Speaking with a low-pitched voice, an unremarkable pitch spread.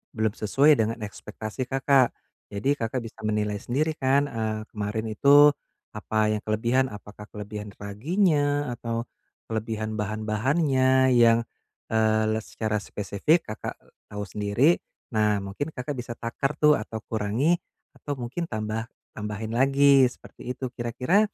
Yes: low, 115 Hz; average, 4.1 semitones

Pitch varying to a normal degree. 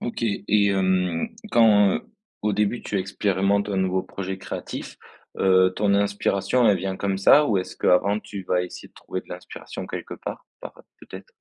No: narrow, 1.7 semitones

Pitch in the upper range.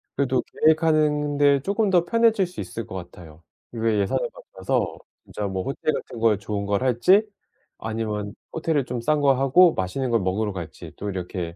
No: low, 120 Hz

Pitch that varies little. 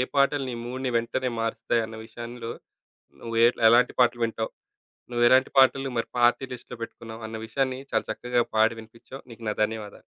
Yes: narrow, 2.2 semitones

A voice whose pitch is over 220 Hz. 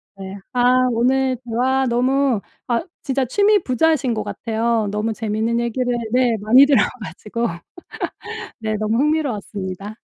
Yes: high, 235 Hz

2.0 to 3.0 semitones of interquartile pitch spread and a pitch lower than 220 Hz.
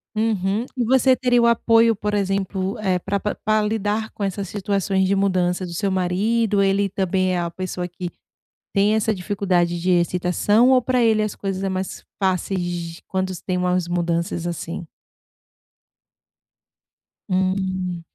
Yes: narrow, 2.5 semitones; high, 190 Hz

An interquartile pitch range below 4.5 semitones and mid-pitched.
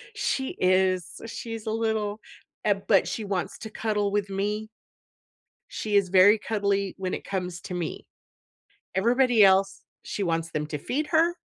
No: average, 2.8 semitones; high, 200 Hz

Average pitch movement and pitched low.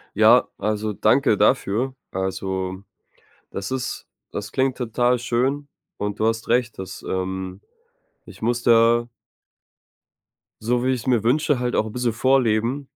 Yes: average, 3.3 semitones; low, 115 Hz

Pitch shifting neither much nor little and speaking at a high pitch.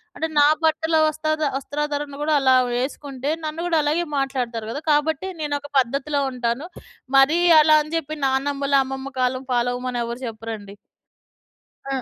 Yes: average, 3.1 semitones; very high, 280 Hz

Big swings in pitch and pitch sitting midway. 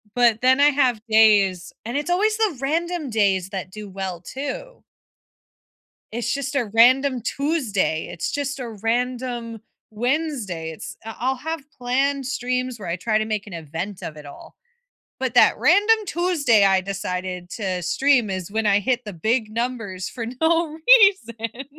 No: wide, 5.7 semitones; high, 235 Hz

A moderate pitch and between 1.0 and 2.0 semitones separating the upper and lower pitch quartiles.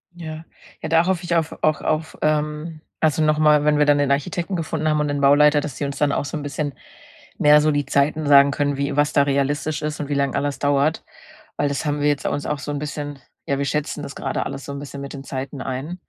Yes: medium, 145 Hz; narrow, 1.4 semitones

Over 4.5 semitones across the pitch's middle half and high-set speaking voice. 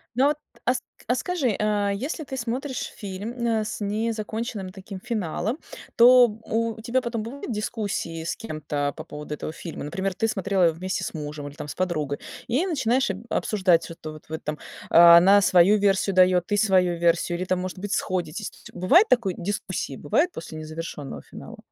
Yes: average, 5.2 semitones; high, 195 Hz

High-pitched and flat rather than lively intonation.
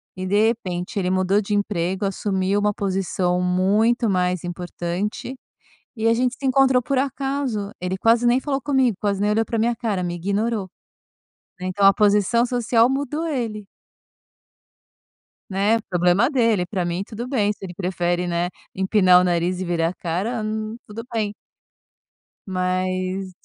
No: high, 200 Hz; average, 4.0 semitones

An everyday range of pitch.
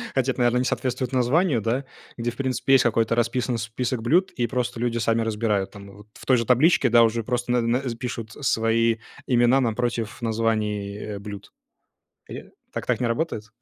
No: narrow, 1.9 semitones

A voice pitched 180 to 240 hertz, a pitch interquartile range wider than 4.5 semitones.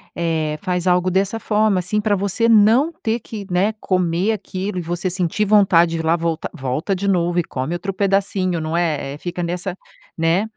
No: medium, 185 Hz; average, 3.1 semitones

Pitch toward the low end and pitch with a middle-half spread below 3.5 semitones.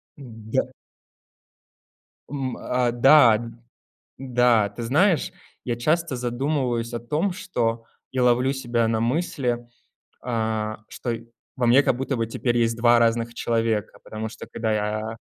Yes: low, 120 Hz; narrow, 2.4 semitones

